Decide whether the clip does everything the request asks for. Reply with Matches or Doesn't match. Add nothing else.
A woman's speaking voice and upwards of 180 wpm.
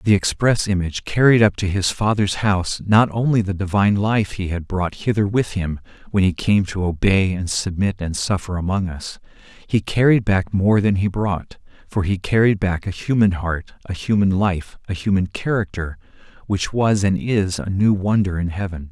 Doesn't match